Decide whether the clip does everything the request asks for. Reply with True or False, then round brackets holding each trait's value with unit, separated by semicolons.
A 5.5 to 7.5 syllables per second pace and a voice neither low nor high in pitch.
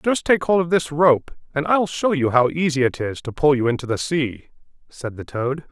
False (5.0 syllables/s; 145 Hz)